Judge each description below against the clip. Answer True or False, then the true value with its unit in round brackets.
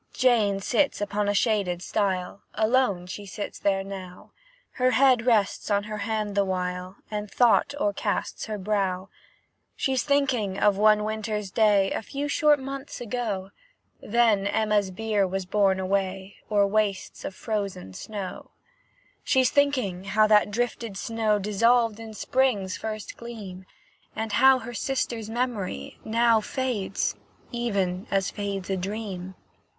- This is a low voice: False (210 Hz)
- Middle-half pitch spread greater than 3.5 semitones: False (3.2 semitones)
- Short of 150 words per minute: True (140 wpm)